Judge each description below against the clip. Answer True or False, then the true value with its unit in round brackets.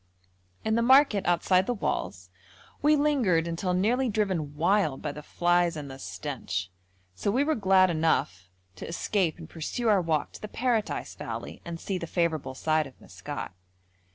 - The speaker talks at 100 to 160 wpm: False (170 wpm)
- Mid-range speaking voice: True (175 Hz)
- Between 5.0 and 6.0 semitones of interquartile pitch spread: True (5.4 semitones)